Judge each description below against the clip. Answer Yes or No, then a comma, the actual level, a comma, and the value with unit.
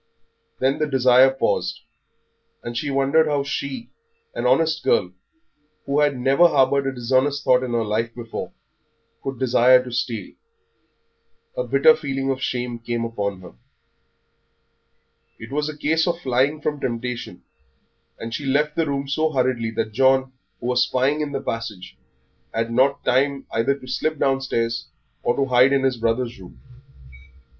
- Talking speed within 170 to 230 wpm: No, average, 155 wpm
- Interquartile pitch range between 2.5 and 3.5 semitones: Yes, average, 2.9 semitones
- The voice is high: No, low, 130 Hz